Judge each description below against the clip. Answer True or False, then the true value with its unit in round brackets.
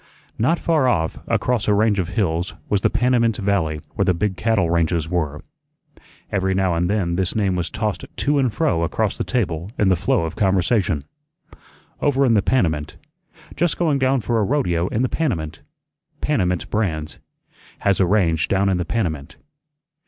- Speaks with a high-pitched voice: False (95 Hz)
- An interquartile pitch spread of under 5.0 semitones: False (5.3 semitones)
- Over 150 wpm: True (175 wpm)